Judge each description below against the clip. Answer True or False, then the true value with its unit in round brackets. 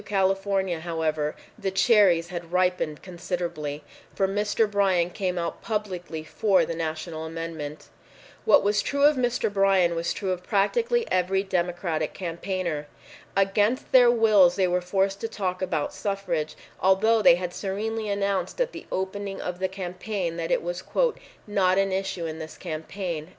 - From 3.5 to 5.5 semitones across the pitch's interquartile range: False (2.9 semitones)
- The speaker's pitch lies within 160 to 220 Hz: True (185 Hz)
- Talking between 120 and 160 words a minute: True (155 wpm)